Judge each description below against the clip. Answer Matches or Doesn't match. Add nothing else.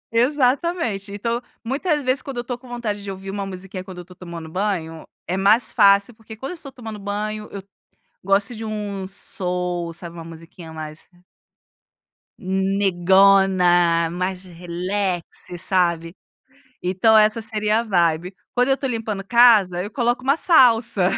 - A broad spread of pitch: Doesn't match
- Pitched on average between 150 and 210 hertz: Matches